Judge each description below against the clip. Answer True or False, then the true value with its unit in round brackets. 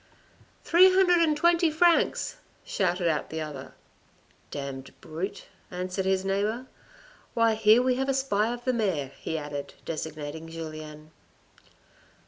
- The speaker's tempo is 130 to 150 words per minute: True (145 wpm)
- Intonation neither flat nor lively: False (8.8 semitones)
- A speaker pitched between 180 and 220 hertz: True (190 Hz)